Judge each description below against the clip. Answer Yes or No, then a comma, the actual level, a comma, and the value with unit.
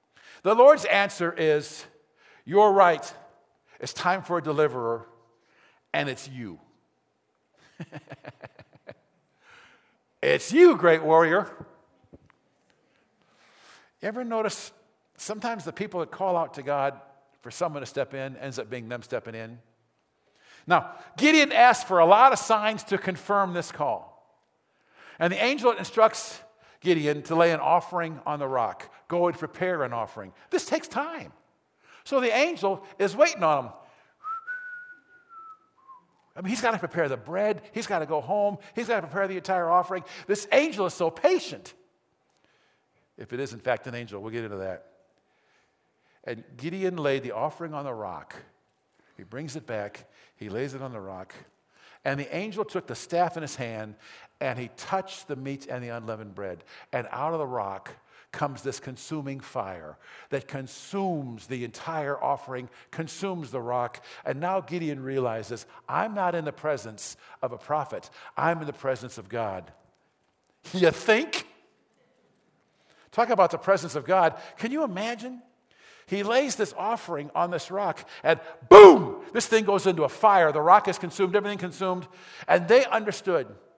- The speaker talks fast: No, average, 160 wpm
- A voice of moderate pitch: Yes, medium, 170 Hz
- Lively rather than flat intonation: Yes, wide, 7.5 semitones